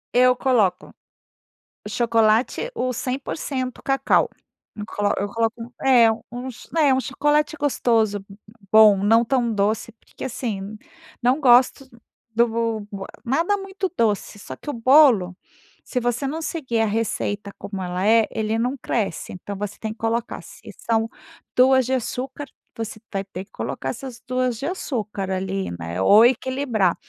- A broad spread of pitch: No, average, 3.7 semitones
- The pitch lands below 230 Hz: No, high, 235 Hz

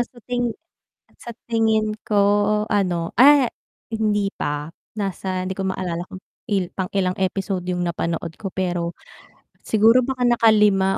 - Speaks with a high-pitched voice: Yes, high, 195 Hz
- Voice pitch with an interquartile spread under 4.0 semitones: Yes, average, 3.5 semitones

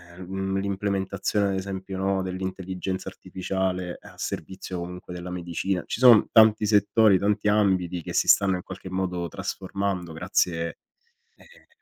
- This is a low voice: Yes, very low, 95 Hz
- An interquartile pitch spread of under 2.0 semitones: Yes, narrow, 1.5 semitones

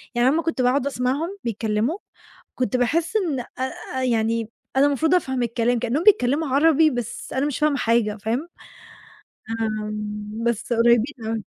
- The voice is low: No, very high, 250 Hz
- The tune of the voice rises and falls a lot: No, average, 4.2 semitones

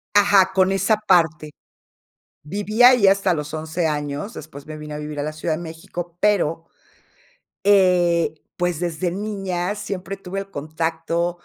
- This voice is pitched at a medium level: Yes, medium, 175 Hz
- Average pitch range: Yes, average, 3.8 semitones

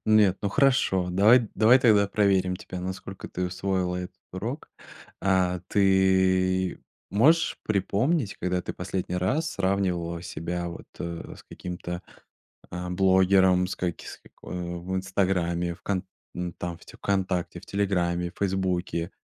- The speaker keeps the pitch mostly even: Yes, narrow, 1.7 semitones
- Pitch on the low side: Yes, very low, 95 Hz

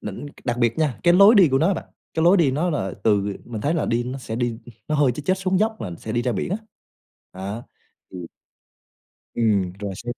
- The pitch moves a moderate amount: No, wide, 7.1 semitones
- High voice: No, low, 125 Hz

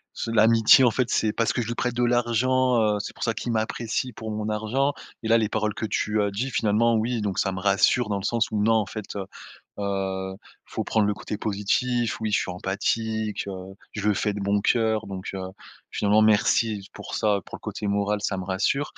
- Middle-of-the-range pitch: No, low, 110 Hz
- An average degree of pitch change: No, narrow, 2.3 semitones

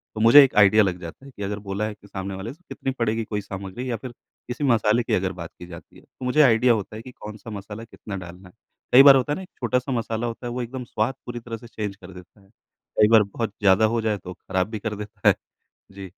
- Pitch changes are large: No, average, 3.5 semitones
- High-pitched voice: No, low, 110 Hz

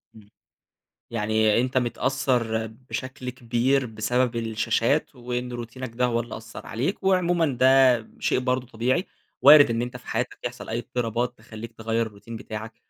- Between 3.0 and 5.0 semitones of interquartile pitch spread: No, narrow, 2.4 semitones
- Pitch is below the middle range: Yes, low, 120 Hz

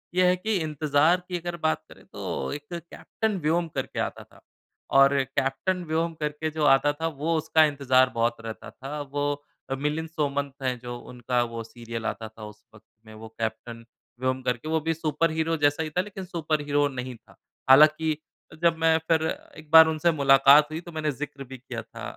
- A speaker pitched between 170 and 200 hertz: No, medium, 145 Hz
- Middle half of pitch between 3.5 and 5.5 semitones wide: Yes, average, 3.8 semitones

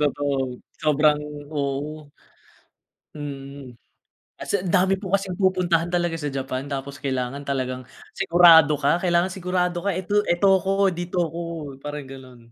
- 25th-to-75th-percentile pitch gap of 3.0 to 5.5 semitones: Yes, average, 4.5 semitones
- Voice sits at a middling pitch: Yes, medium, 160 Hz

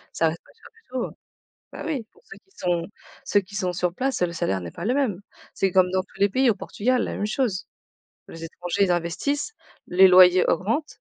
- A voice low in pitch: No, high, 190 Hz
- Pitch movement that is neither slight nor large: No, wide, 6.2 semitones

